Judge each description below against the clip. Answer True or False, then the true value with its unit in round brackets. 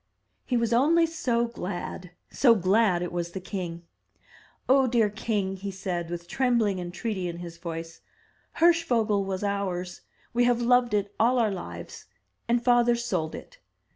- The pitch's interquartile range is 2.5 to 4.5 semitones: False (5.2 semitones)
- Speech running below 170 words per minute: True (160 wpm)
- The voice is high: True (205 Hz)